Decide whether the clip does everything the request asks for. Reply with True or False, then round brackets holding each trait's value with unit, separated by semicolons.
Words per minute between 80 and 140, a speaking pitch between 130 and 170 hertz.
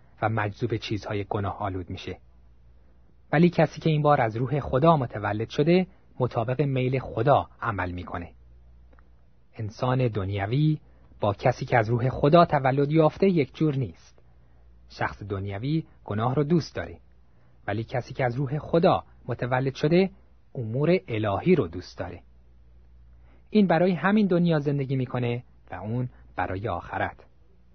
False (135 wpm; 115 Hz)